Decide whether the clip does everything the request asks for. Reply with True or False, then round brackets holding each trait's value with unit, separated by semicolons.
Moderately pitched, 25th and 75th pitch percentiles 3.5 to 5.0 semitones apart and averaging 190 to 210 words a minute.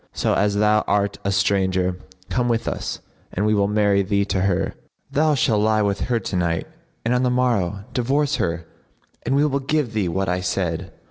False (105 Hz; 4.3 semitones; 200 wpm)